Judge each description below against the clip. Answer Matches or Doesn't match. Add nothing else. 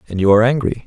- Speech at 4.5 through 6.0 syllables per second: Doesn't match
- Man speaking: Matches